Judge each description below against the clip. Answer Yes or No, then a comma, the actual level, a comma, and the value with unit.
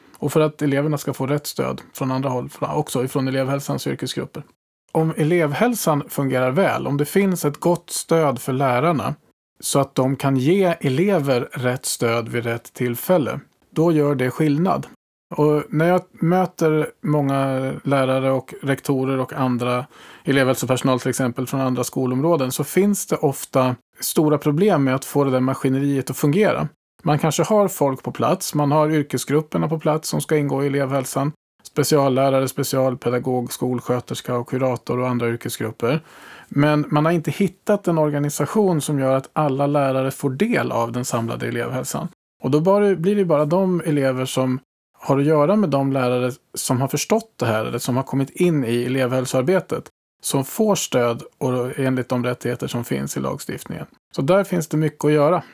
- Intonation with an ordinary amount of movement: Yes, average, 3.1 semitones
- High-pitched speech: No, medium, 140 Hz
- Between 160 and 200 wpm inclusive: Yes, average, 170 wpm